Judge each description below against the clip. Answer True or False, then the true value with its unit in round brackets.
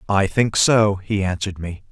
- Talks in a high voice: False (100 Hz)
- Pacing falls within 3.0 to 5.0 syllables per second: True (4.8 syllables/s)